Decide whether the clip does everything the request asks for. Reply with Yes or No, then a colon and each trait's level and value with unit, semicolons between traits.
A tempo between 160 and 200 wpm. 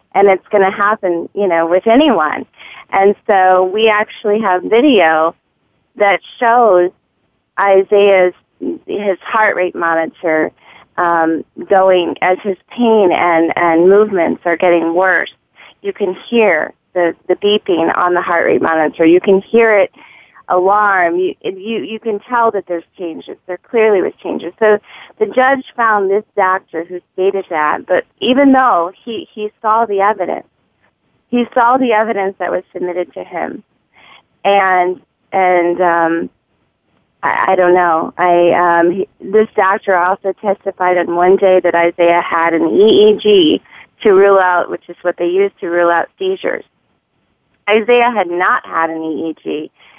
No: average, 150 wpm